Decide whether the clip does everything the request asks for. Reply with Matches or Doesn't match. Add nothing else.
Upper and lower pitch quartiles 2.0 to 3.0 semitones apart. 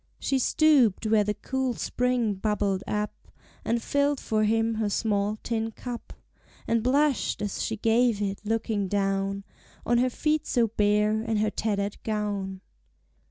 Matches